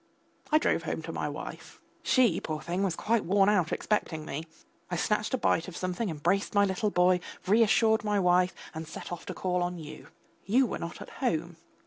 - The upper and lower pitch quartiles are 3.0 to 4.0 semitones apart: Yes, average, 3.6 semitones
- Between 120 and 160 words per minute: No, average, 200 wpm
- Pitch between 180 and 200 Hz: Yes, medium, 185 Hz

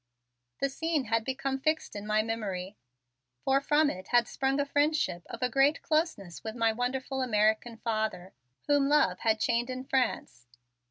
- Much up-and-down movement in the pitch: No, average, 4.1 semitones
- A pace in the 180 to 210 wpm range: No, average, 165 wpm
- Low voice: No, high, 245 Hz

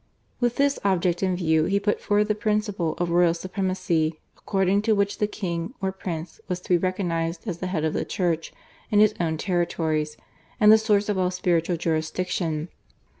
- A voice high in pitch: No, medium, 180 Hz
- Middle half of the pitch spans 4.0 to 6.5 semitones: No, average, 3.4 semitones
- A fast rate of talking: No, average, 185 wpm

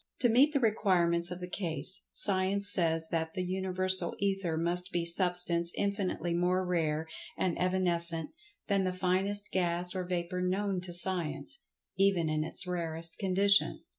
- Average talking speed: Yes, average, 150 wpm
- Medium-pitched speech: Yes, medium, 180 Hz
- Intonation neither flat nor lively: No, narrow, 2.0 semitones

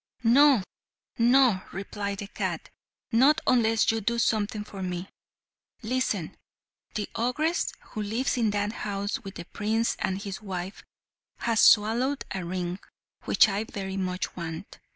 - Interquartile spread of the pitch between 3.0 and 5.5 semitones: Yes, average, 3.3 semitones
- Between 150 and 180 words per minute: No, average, 140 wpm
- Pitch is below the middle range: No, high, 210 Hz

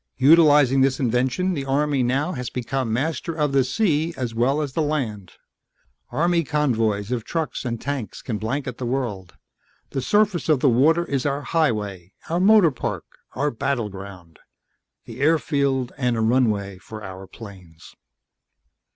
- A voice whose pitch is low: Yes, low, 130 Hz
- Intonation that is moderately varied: Yes, average, 4.9 semitones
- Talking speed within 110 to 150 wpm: Yes, average, 145 wpm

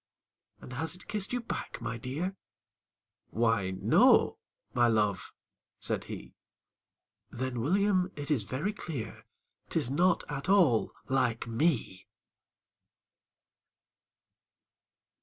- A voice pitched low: Yes, low, 130 Hz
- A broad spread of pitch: Yes, wide, 7.6 semitones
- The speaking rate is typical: No, slow, 100 wpm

